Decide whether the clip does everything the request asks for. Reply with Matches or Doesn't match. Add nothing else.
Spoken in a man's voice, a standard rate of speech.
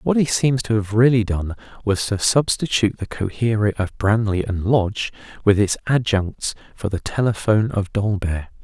Matches